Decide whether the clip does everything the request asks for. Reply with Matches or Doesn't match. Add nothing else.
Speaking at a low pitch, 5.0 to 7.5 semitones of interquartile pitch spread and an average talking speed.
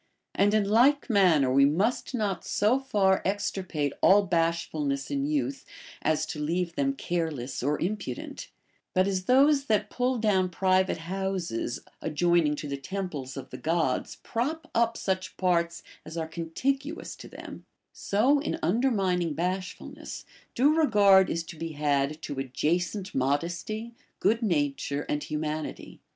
Doesn't match